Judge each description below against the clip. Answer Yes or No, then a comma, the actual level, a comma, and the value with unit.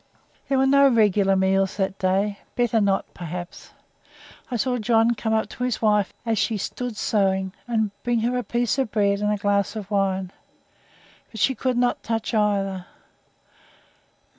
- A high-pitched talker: Yes, high, 210 Hz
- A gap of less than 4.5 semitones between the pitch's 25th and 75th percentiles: Yes, average, 3.4 semitones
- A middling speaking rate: Yes, average, 165 wpm